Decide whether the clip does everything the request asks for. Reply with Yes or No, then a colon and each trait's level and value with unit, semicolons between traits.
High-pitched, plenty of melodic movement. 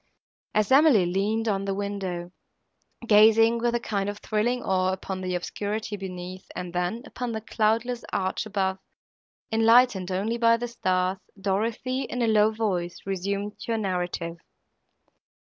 No: high, 205 Hz; average, 3.3 semitones